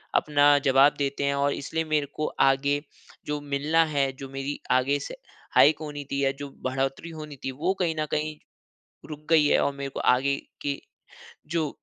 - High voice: No, medium, 145 Hz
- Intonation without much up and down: Yes, narrow, 1.8 semitones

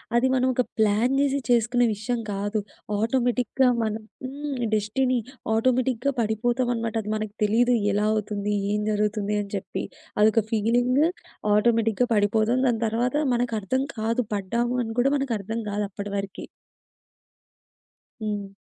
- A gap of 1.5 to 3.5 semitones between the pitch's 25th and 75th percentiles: Yes, average, 2.9 semitones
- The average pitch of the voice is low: No, high, 225 Hz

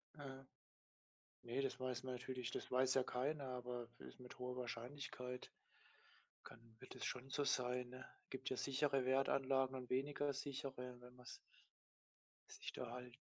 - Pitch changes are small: Yes, narrow, 1.3 semitones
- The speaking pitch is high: No, low, 130 Hz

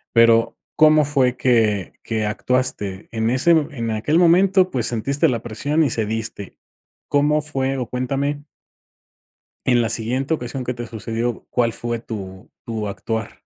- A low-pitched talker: Yes, low, 120 Hz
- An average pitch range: Yes, average, 4.1 semitones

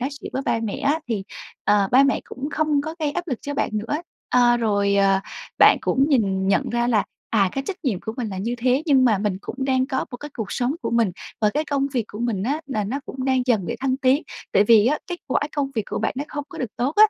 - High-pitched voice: Yes, high, 245 Hz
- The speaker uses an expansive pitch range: No, average, 4.5 semitones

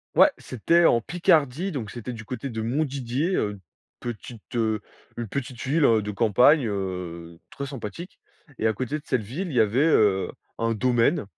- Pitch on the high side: No, low, 120 Hz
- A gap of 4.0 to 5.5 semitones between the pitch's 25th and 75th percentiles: Yes, average, 4.5 semitones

